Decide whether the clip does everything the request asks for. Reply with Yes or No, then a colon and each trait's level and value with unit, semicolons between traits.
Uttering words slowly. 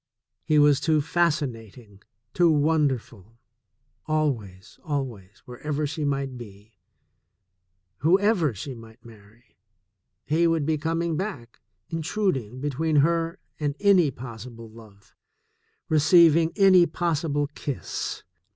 Yes: slow, 110 wpm